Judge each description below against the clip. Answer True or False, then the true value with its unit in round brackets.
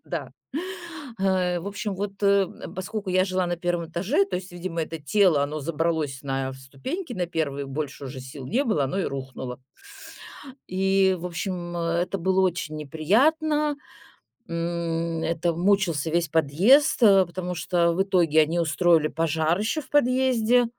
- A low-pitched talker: False (175 Hz)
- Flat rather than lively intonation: False (3.7 semitones)